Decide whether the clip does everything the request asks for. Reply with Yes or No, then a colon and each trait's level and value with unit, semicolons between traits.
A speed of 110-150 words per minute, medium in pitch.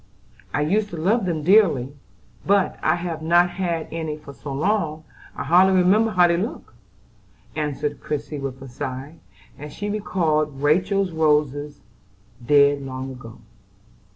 Yes: average, 145 wpm; medium, 155 Hz